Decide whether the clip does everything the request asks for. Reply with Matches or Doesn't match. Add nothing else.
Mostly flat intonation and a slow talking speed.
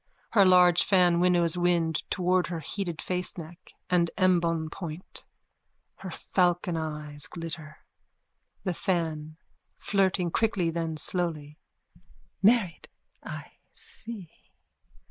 Matches